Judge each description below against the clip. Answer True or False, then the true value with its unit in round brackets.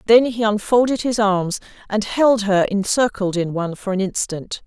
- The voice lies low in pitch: False (210 Hz)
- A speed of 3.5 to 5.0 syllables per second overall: True (4.8 syllables/s)